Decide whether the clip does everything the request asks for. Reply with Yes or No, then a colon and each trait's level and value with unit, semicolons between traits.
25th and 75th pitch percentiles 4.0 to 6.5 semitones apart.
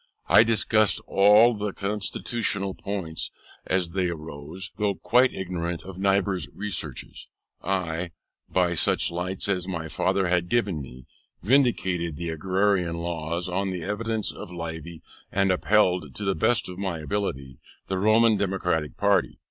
No: average, 3.1 semitones